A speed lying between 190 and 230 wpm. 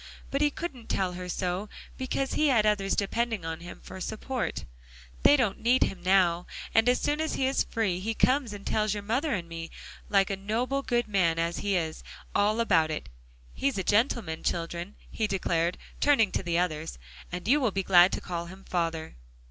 Yes: average, 200 wpm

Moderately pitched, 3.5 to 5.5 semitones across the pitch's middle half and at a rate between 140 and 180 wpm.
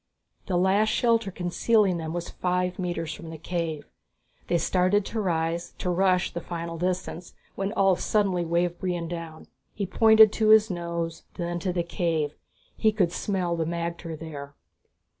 No: medium, 175 Hz; narrow, 2.4 semitones; average, 160 wpm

